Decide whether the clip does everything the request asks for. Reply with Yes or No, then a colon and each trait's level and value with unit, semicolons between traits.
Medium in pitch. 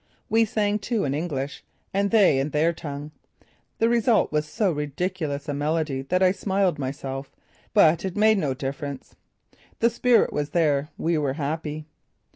Yes: medium, 155 Hz